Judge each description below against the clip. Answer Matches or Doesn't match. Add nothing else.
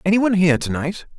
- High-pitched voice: Doesn't match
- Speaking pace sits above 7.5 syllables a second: Matches